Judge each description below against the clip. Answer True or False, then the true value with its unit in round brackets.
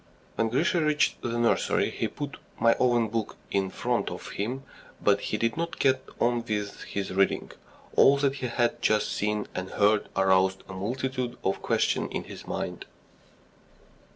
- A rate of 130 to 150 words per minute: False (165 wpm)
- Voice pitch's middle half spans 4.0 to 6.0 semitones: True (4.5 semitones)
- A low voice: True (115 Hz)